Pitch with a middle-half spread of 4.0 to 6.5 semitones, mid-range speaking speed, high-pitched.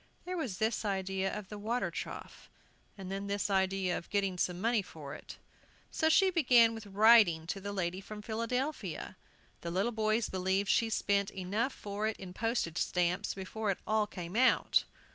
No: average, 2.9 semitones; average, 180 wpm; high, 200 Hz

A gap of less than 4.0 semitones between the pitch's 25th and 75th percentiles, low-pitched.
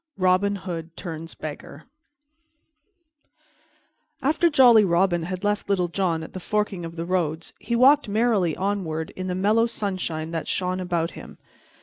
No: average, 3.6 semitones; medium, 185 Hz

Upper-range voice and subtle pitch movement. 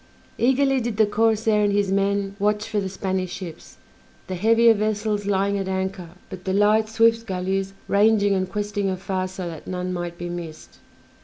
Yes: high, 200 Hz; narrow, 2.3 semitones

